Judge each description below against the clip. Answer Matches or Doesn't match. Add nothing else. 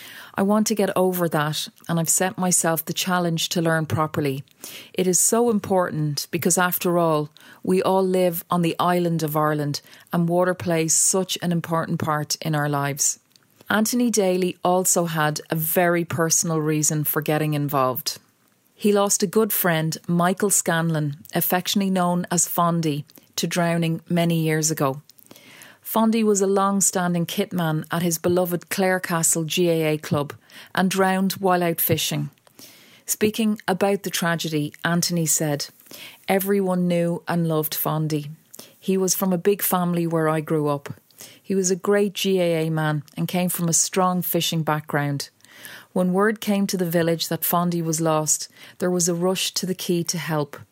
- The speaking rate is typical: Matches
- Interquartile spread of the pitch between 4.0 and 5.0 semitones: Doesn't match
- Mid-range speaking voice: Matches